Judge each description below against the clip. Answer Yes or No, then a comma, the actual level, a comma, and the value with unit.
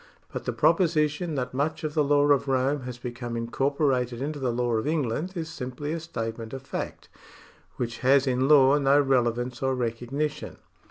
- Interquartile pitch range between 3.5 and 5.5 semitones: No, average, 3.1 semitones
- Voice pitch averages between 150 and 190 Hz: No, low, 135 Hz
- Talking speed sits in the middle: Yes, average, 175 wpm